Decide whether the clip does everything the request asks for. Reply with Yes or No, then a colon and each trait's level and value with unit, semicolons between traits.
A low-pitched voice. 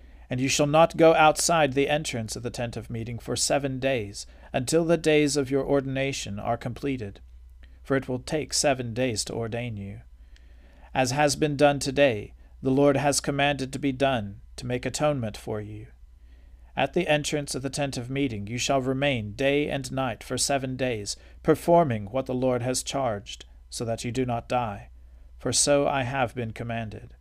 Yes: low, 130 Hz